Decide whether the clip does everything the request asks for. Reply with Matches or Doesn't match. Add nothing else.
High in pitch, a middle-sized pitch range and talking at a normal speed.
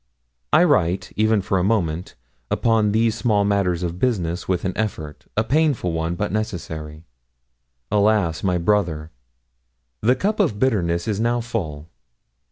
Doesn't match